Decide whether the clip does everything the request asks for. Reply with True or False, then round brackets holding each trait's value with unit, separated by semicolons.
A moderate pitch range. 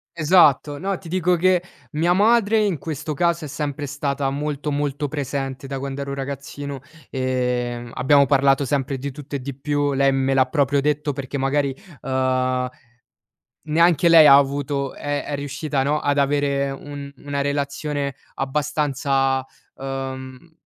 False (1.8 semitones)